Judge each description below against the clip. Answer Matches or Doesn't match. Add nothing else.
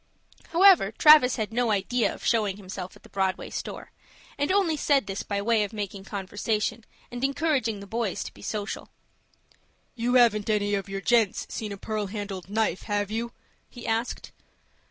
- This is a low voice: Doesn't match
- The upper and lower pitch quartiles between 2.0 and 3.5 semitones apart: Matches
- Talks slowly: Doesn't match